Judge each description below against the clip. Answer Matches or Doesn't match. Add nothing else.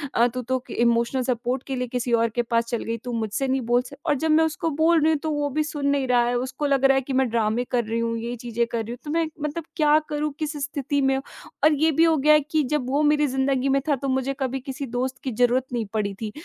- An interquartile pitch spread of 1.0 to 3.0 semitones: Doesn't match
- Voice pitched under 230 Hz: Doesn't match